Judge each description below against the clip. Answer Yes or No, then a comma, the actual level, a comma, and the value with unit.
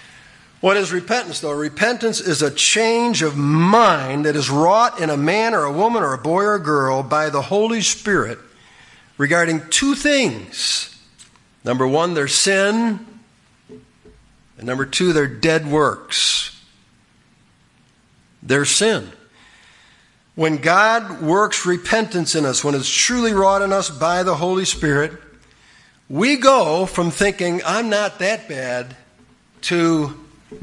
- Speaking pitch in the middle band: Yes, medium, 170 Hz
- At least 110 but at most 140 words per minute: Yes, slow, 135 wpm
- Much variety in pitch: Yes, wide, 6.2 semitones